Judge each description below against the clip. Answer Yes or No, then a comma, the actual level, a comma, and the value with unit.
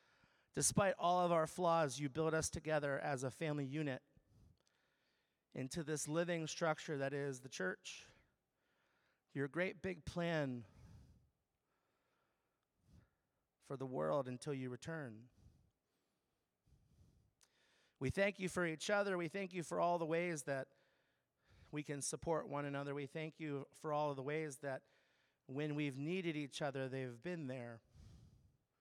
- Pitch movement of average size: Yes, average, 3.6 semitones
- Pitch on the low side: No, medium, 150 Hz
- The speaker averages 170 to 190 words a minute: No, average, 140 wpm